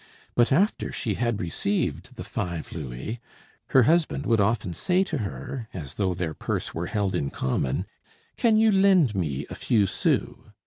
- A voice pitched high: No, low, 105 Hz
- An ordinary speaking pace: Yes, average, 170 wpm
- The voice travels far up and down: Yes, wide, 8.4 semitones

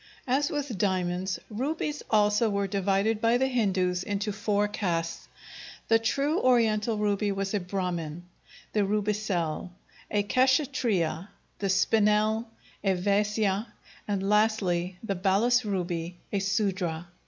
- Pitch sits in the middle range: No, high, 205 Hz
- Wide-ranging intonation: No, average, 2.8 semitones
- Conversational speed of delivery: No, slow, 120 wpm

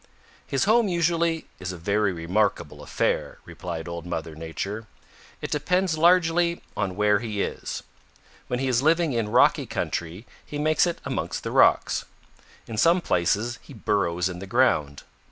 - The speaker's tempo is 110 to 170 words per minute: Yes, average, 155 wpm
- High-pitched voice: No, low, 110 Hz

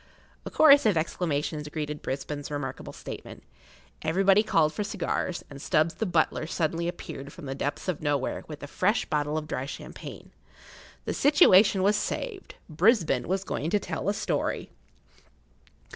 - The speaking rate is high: No, average, 160 wpm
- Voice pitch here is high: No, medium, 160 Hz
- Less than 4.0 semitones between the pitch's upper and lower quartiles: No, average, 4.8 semitones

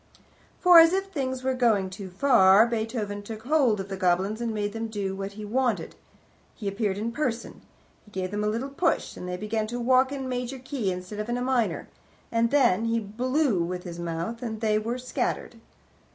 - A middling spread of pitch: Yes, average, 4.1 semitones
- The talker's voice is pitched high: Yes, high, 225 Hz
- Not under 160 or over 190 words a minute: No, fast, 205 wpm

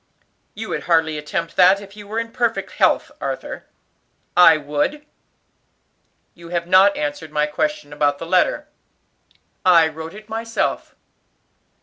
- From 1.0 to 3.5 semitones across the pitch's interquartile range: No, wide, 5.4 semitones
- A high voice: No, medium, 175 Hz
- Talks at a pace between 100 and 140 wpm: Yes, slow, 135 wpm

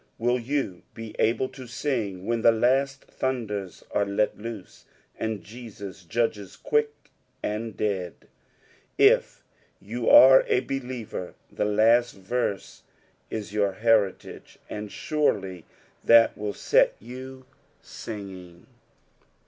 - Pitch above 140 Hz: No, low, 110 Hz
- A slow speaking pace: Yes, slow, 115 wpm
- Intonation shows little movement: No, average, 3.5 semitones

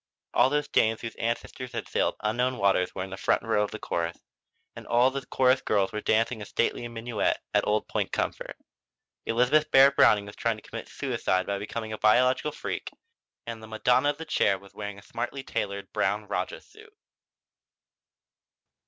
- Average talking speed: Yes, average, 185 wpm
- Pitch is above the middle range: No, low, 115 Hz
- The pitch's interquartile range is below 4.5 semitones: Yes, average, 3.8 semitones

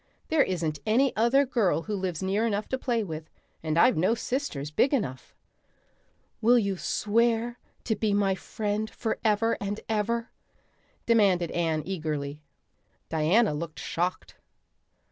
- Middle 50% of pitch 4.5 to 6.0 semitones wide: Yes, wide, 5.6 semitones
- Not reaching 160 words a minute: Yes, slow, 135 wpm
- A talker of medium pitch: No, high, 205 Hz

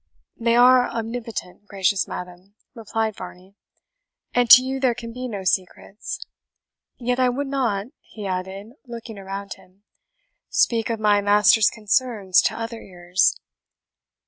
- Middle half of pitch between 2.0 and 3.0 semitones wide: No, average, 3.5 semitones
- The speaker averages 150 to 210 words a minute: No, slow, 135 wpm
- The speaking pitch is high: Yes, high, 215 Hz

